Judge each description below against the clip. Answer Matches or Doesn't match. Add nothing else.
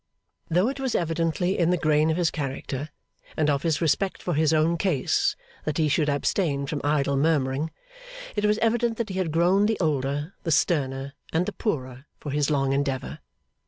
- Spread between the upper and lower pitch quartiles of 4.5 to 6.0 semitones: Doesn't match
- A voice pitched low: Doesn't match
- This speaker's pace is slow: Doesn't match